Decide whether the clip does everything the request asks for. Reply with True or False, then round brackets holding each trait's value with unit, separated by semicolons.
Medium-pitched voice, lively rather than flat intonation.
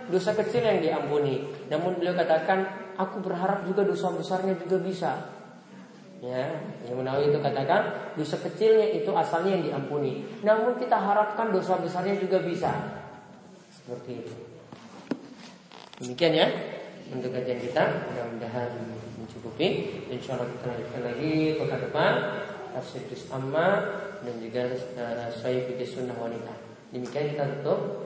True (155 Hz; 7.4 semitones)